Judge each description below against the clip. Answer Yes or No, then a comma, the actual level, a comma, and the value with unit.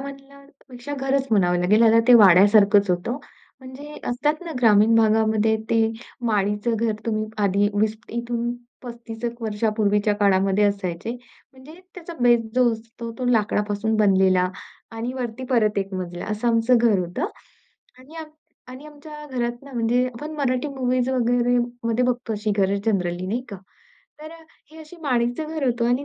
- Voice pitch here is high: Yes, high, 230 Hz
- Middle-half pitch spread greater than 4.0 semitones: No, average, 3.6 semitones